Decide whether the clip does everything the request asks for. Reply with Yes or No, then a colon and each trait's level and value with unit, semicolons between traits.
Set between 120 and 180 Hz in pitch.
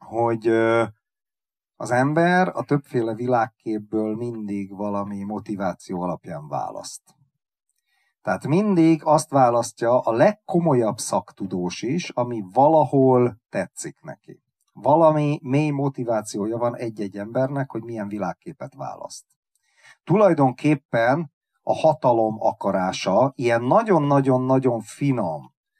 Yes: low, 125 Hz